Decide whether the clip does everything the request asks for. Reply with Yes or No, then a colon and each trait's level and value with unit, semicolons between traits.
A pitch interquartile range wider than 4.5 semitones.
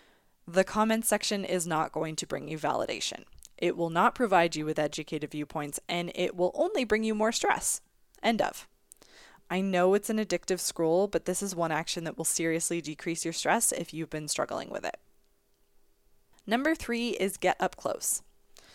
No: average, 4.1 semitones